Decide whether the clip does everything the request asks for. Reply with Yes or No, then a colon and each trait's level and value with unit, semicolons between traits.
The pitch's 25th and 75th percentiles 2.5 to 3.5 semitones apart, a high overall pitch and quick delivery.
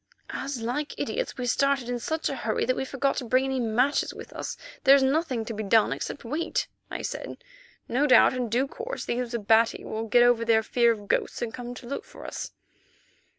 Yes: average, 3.0 semitones; high, 245 Hz; fast, 215 wpm